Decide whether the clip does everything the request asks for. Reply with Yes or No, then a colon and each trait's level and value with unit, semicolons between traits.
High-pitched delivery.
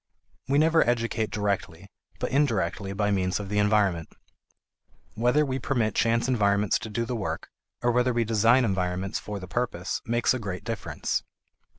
No: low, 110 Hz